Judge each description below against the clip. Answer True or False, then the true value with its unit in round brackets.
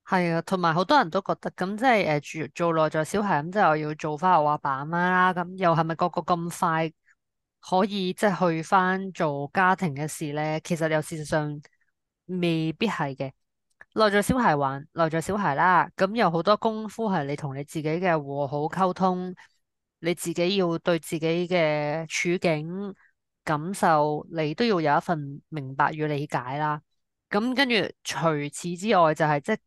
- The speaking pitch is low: False (170 Hz)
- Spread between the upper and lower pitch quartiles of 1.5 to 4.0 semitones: True (3.4 semitones)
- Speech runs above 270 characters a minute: False (260 characters per minute)